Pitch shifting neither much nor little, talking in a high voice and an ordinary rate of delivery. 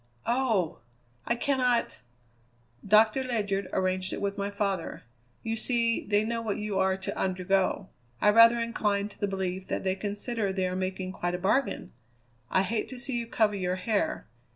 Yes: average, 3.5 semitones; high, 200 Hz; average, 175 wpm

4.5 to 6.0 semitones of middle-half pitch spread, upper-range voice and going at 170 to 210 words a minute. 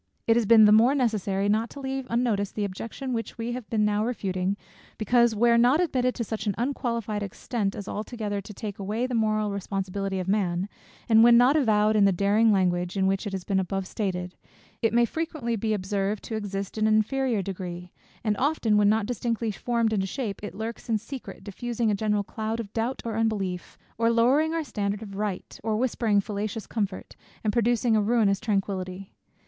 No: average, 2.8 semitones; high, 215 Hz; average, 200 wpm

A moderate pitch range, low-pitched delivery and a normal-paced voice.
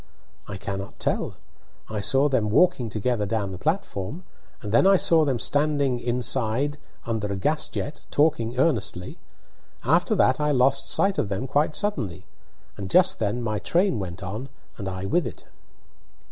No: wide, 6.3 semitones; low, 125 Hz; average, 160 wpm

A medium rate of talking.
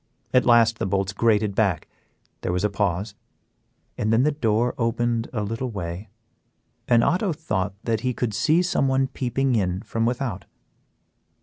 Yes: average, 160 wpm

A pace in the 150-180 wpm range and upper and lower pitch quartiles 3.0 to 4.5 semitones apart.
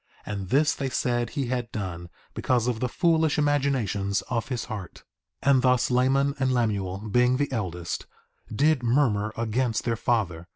Yes: average, 165 wpm; average, 4.1 semitones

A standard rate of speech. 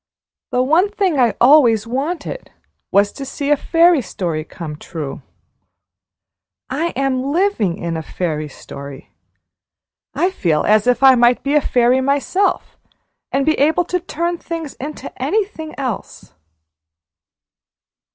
No: slow, 130 wpm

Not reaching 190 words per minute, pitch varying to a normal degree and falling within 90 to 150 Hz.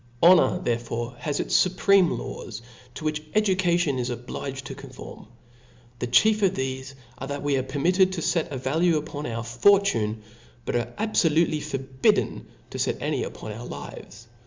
No: average, 165 wpm; wide, 6.1 semitones; medium, 140 Hz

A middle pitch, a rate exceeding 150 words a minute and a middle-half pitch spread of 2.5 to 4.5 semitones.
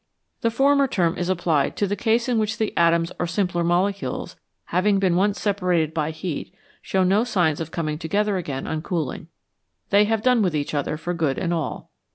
Yes: medium, 180 Hz; average, 200 wpm; average, 4.1 semitones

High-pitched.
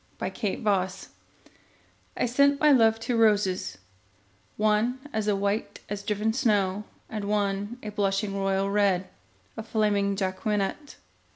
Yes: high, 210 Hz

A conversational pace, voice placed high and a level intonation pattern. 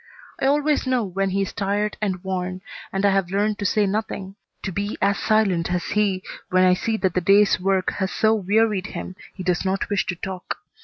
No: fast, 215 wpm; high, 195 Hz; narrow, 2.0 semitones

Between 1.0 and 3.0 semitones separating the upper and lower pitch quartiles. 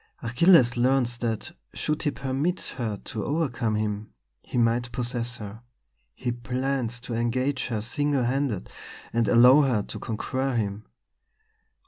Yes: average, 2.7 semitones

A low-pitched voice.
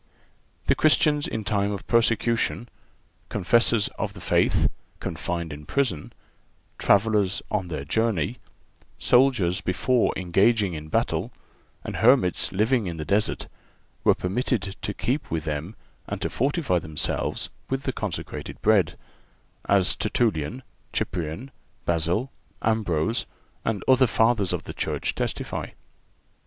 Yes: low, 105 Hz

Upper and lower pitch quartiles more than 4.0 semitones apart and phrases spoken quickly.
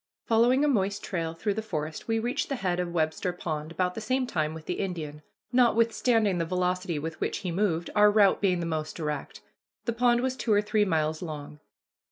Yes: wide, 5.5 semitones; fast, 210 wpm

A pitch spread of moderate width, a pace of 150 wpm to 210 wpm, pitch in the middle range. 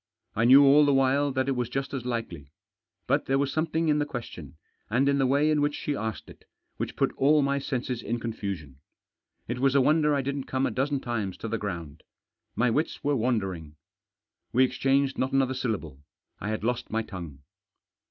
No: average, 4.1 semitones; fast, 205 wpm; low, 130 Hz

